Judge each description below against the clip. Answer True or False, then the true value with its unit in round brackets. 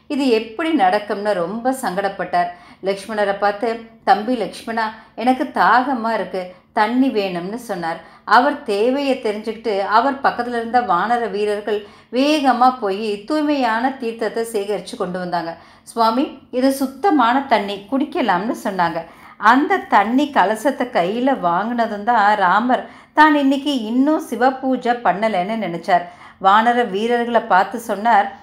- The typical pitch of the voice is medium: False (225 Hz)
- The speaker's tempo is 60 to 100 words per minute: False (115 wpm)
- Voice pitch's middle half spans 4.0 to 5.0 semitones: True (4.3 semitones)